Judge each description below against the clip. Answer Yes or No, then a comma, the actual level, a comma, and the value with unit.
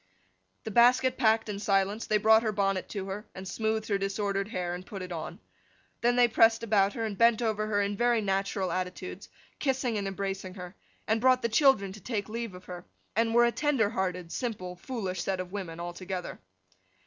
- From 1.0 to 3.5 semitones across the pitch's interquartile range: Yes, average, 3.2 semitones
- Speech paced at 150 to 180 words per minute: No, average, 200 wpm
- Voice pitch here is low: No, high, 205 Hz